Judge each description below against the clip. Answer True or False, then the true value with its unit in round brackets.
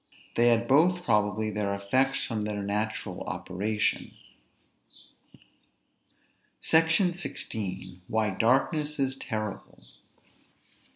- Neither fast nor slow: False (90 wpm)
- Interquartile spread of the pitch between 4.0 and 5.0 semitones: True (4.6 semitones)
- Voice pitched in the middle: False (110 Hz)